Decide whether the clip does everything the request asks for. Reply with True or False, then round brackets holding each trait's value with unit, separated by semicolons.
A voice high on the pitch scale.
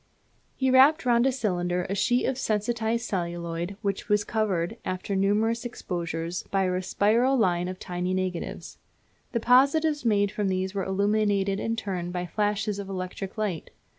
True (200 Hz)